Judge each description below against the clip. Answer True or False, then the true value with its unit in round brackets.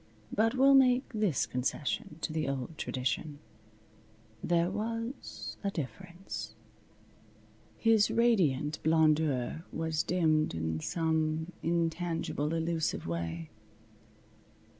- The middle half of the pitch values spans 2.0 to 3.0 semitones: False (4.7 semitones)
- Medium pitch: True (160 Hz)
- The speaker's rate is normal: False (95 wpm)